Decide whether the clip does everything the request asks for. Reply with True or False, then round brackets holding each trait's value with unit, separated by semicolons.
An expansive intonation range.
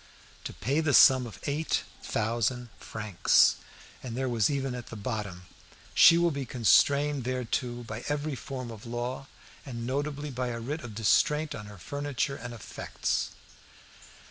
False (3.5 semitones)